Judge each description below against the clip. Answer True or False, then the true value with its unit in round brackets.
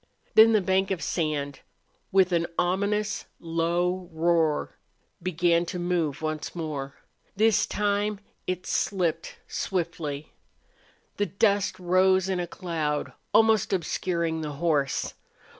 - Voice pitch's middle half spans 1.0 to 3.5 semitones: True (3.0 semitones)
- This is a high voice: False (175 Hz)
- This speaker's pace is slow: True (115 wpm)